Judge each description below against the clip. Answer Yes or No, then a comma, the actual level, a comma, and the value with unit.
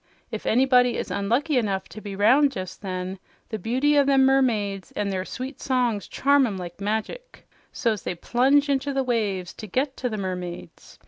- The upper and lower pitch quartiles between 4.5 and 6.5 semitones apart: Yes, average, 5.3 semitones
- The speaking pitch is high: Yes, high, 230 Hz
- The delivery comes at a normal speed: Yes, average, 185 wpm